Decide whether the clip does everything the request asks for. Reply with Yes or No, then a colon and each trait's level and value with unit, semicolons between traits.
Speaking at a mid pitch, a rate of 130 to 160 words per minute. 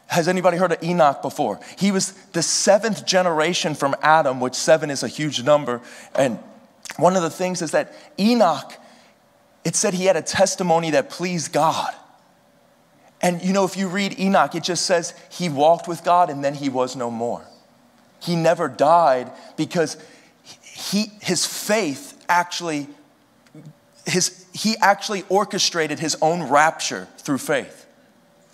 Yes: medium, 175 Hz; average, 155 wpm